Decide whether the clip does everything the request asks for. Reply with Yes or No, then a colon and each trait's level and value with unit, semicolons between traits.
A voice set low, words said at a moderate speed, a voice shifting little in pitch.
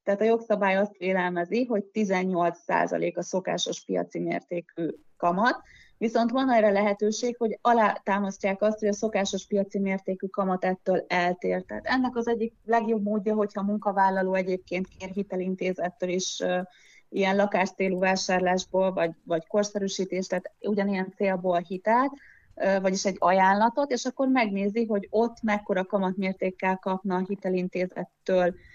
No: high, 195 Hz; average, 135 wpm; narrow, 2.3 semitones